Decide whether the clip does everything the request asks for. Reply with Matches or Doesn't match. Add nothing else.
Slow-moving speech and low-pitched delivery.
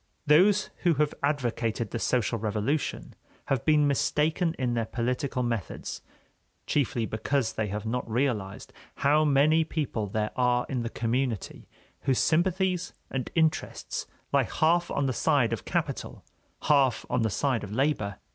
Doesn't match